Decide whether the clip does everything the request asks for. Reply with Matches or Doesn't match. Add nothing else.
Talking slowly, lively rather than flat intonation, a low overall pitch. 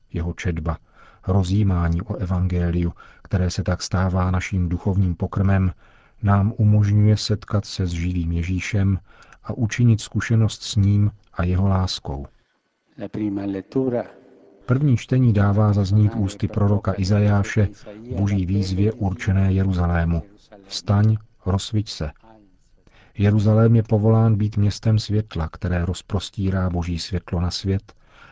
Doesn't match